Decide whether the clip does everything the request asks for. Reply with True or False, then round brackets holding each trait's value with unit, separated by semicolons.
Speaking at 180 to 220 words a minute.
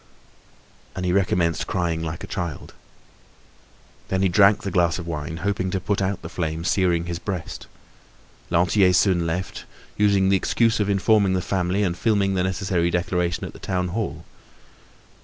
False (165 wpm)